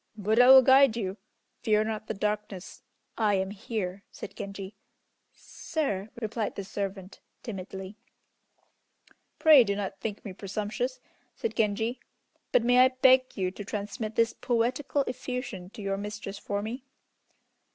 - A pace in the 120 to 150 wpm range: Yes, average, 140 wpm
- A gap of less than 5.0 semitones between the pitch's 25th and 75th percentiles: Yes, average, 3.6 semitones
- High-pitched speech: Yes, high, 215 Hz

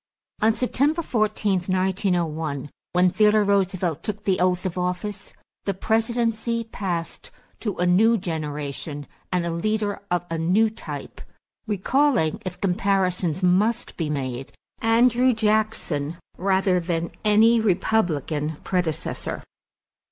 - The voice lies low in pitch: No, high, 190 Hz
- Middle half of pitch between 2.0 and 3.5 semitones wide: No, average, 4.2 semitones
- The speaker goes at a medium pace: No, slow, 120 wpm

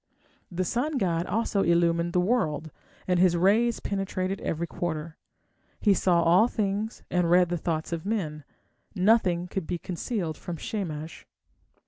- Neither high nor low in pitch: Yes, medium, 180 Hz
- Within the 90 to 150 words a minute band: Yes, average, 145 wpm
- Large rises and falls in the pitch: No, average, 3.0 semitones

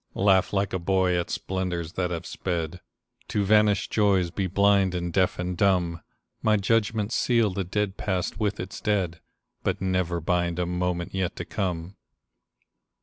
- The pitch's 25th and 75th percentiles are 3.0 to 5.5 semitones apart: No, narrow, 2.4 semitones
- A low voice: Yes, very low, 95 Hz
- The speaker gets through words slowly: No, average, 160 wpm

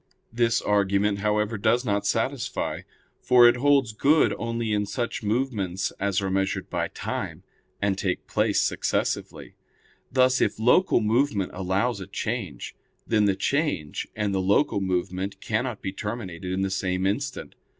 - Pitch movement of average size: Yes, average, 3.7 semitones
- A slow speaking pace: No, average, 150 wpm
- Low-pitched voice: Yes, low, 105 Hz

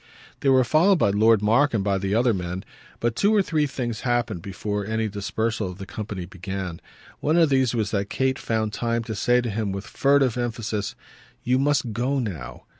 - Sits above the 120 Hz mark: No, low, 115 Hz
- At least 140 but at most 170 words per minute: No, average, 200 wpm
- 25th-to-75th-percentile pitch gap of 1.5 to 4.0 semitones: No, average, 4.4 semitones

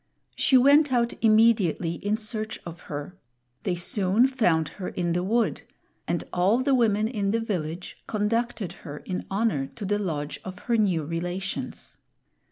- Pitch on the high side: Yes, high, 200 Hz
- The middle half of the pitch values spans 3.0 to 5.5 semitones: Yes, average, 4.5 semitones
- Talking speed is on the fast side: No, average, 160 wpm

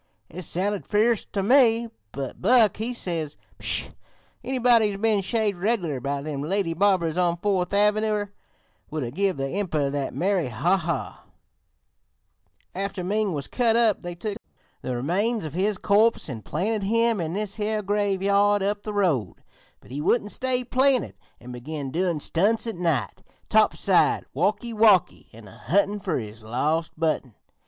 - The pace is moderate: Yes, average, 165 wpm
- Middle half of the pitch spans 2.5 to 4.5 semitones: No, average, 5.3 semitones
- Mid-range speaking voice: No, high, 195 Hz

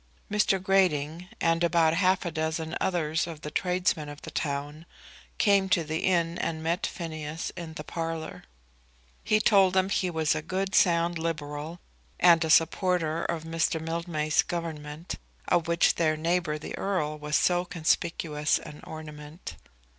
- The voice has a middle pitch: Yes, medium, 165 Hz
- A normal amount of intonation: No, narrow, 2.2 semitones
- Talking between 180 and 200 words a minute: No, average, 155 wpm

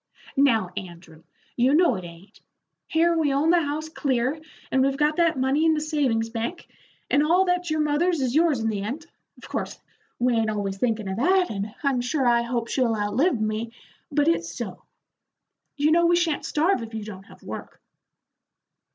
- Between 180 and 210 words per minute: Yes, average, 190 wpm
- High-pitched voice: Yes, very high, 270 Hz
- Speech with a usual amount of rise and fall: No, wide, 5.9 semitones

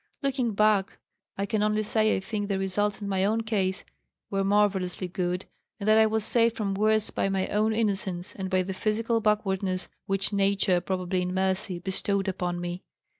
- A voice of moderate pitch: No, high, 195 Hz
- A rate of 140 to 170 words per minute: No, average, 185 wpm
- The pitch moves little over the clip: Yes, narrow, 2.2 semitones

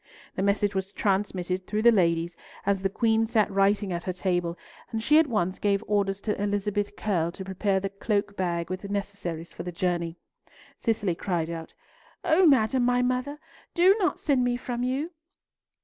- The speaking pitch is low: No, high, 200 Hz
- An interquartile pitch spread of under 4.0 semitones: Yes, average, 3.6 semitones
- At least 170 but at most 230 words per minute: Yes, average, 180 wpm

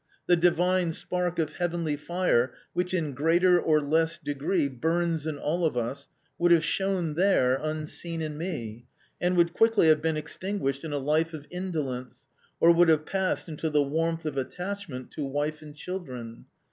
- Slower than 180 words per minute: Yes, average, 170 wpm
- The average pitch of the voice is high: No, medium, 160 Hz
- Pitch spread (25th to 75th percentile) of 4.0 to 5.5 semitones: No, average, 3.2 semitones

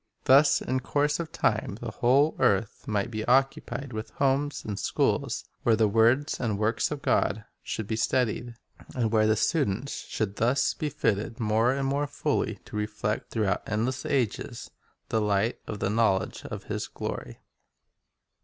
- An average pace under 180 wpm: Yes, average, 170 wpm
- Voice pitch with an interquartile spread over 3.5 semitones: Yes, average, 4.0 semitones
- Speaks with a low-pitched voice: Yes, low, 115 Hz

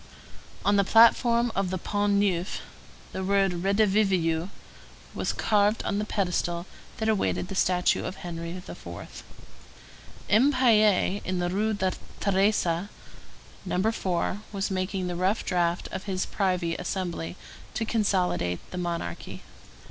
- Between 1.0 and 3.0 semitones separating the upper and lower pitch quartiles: Yes, narrow, 2.6 semitones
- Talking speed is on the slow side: Yes, slow, 130 wpm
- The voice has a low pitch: No, high, 190 Hz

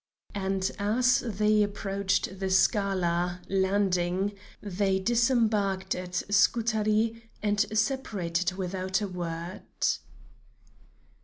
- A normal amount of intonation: No, narrow, 2.3 semitones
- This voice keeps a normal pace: No, slow, 85 wpm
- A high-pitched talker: Yes, high, 195 Hz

